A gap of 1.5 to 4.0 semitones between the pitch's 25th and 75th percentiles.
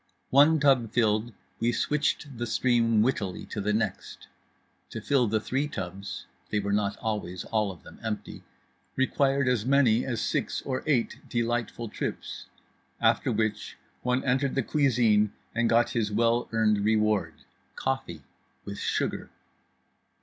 Yes: average, 3.4 semitones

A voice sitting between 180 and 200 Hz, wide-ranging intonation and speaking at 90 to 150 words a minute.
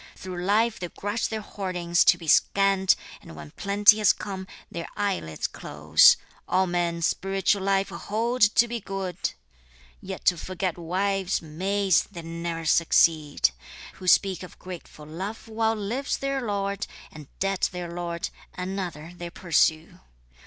No: medium, 185 Hz; average, 2.9 semitones; average, 145 wpm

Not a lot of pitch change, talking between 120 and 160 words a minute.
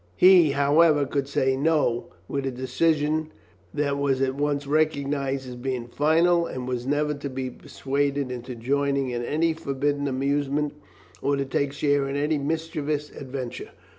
Yes: narrow, 1.9 semitones; average, 155 wpm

